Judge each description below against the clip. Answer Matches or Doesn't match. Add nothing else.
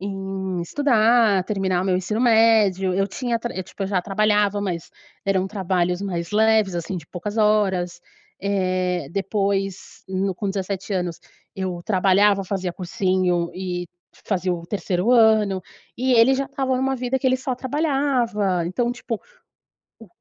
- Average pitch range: Matches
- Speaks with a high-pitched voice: Matches